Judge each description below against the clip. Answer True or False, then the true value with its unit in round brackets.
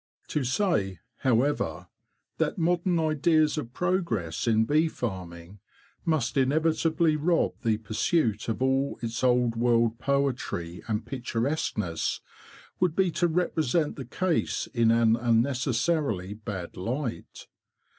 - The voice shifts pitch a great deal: True (5.9 semitones)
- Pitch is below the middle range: True (125 Hz)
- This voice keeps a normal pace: False (115 wpm)